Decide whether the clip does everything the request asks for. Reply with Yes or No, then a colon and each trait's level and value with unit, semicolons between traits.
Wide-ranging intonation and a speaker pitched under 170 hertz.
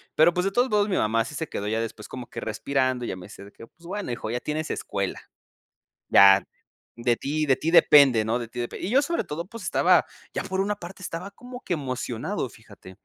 Yes: wide, 8.2 semitones; medium, 140 Hz